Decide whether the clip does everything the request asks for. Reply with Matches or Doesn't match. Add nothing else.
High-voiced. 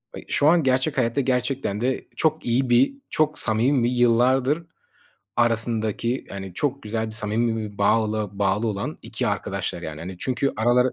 Doesn't match